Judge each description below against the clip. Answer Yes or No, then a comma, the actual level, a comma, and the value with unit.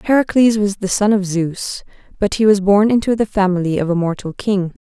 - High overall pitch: Yes, high, 200 Hz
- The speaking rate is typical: No, fast, 210 wpm